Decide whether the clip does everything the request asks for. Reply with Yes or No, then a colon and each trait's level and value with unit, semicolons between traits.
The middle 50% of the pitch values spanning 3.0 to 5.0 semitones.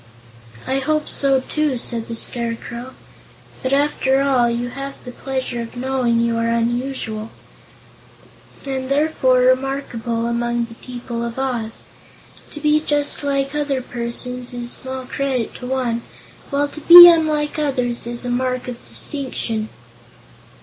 No: narrow, 2.6 semitones